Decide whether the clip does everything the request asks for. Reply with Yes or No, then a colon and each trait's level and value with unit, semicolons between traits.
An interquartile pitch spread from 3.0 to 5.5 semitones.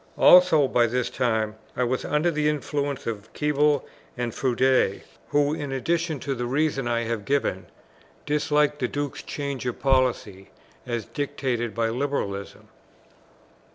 Yes: average, 3.6 semitones